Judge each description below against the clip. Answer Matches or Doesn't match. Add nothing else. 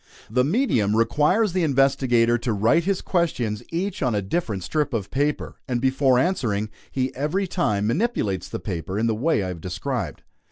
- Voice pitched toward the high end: Doesn't match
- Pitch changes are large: Matches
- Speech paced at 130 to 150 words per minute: Doesn't match